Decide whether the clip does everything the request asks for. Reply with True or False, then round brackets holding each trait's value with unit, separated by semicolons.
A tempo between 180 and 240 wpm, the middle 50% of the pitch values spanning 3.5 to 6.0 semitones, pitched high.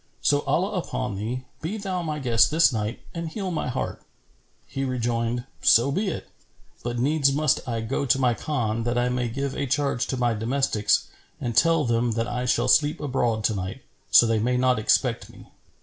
False (195 wpm; 3.9 semitones; 125 Hz)